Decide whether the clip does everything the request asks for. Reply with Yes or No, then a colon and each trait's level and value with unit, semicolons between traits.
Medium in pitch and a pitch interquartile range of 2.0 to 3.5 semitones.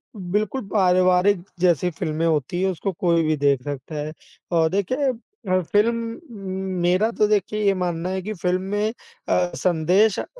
No: medium, 180 Hz; average, 4.0 semitones